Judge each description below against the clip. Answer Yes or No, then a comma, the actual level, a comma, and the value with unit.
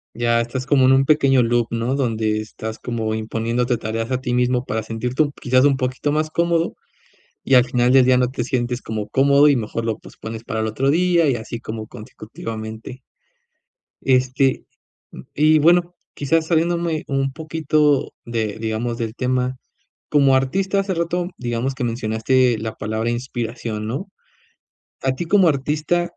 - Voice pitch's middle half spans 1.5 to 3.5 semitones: No, average, 4.1 semitones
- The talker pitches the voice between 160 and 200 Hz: No, low, 125 Hz